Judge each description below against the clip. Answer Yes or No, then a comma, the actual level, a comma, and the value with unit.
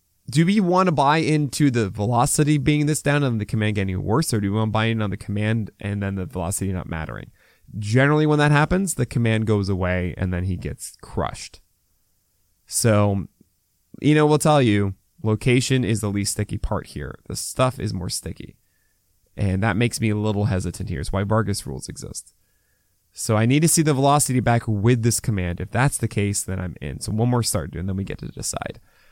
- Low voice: Yes, low, 105 Hz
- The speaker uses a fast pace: Yes, fast, 215 wpm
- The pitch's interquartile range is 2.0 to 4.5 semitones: No, average, 5.0 semitones